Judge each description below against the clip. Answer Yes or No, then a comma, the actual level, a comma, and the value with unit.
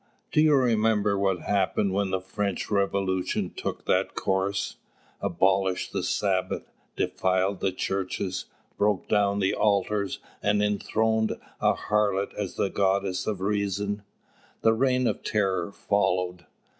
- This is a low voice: Yes, low, 100 Hz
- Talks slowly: Yes, slow, 130 wpm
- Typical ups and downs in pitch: No, narrow, 1.6 semitones